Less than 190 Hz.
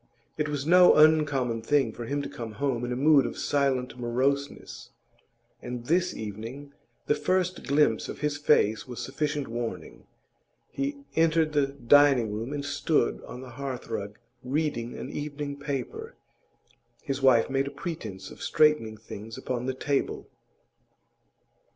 Yes: medium, 140 Hz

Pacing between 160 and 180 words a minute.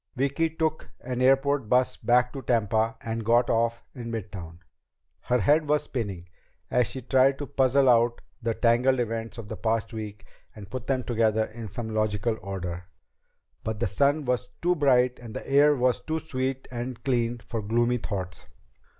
Yes: average, 175 wpm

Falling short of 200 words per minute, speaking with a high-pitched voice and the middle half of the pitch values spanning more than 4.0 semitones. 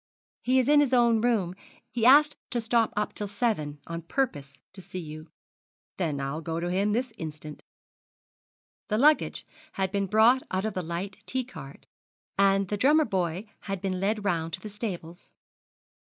Yes: average, 175 wpm; high, 195 Hz; wide, 5.5 semitones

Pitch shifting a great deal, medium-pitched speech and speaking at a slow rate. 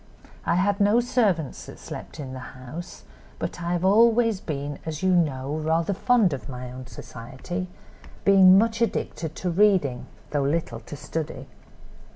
No: wide, 6.1 semitones; medium, 170 Hz; average, 160 wpm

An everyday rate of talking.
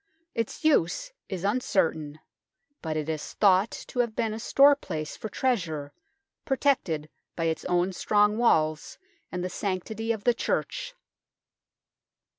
No: slow, 130 wpm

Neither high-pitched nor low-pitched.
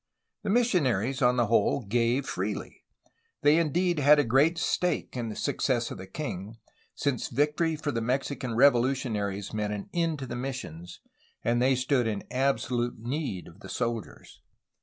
No: low, 125 Hz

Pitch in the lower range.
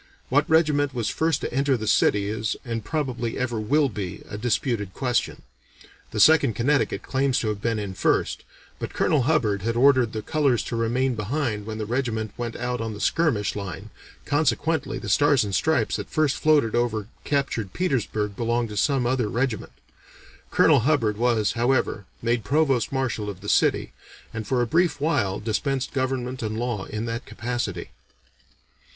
Yes: low, 120 Hz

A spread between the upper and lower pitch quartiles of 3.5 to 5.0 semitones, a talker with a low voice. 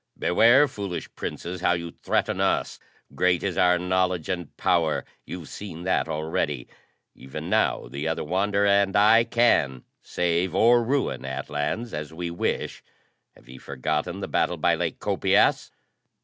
Yes: average, 4.3 semitones; very low, 90 Hz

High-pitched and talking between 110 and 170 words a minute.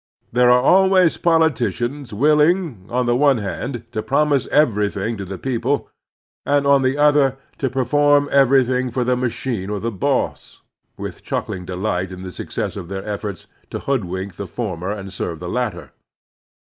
No: low, 125 Hz; average, 160 wpm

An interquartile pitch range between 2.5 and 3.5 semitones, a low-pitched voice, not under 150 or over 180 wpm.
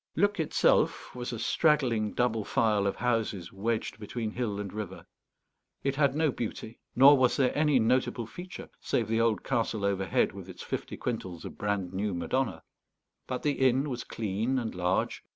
No: average, 4.2 semitones; low, 115 Hz; average, 170 wpm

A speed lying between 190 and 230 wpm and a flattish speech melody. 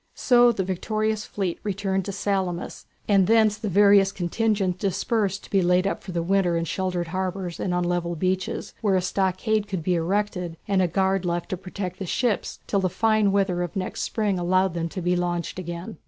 Yes: average, 200 wpm; narrow, 2.3 semitones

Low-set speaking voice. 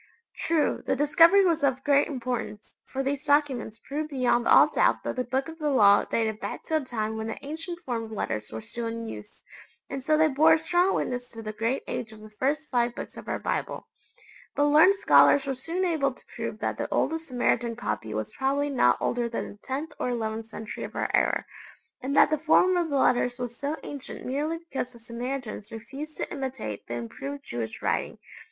No: very high, 265 Hz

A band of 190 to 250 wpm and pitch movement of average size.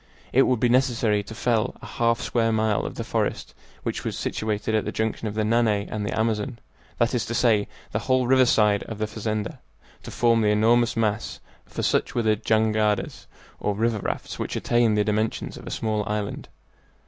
No: average, 200 wpm; narrow, 1.8 semitones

